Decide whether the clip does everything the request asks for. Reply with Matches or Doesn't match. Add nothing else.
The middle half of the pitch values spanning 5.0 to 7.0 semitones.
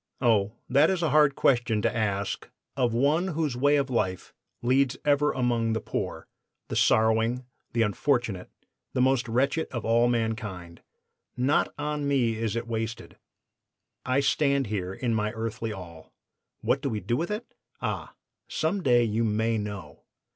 Doesn't match